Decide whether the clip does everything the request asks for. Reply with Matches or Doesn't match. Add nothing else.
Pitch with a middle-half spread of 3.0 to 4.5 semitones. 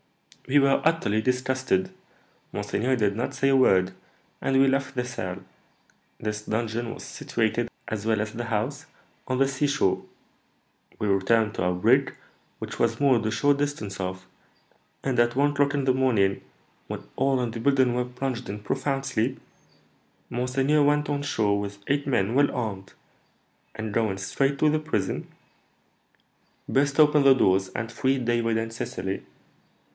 Matches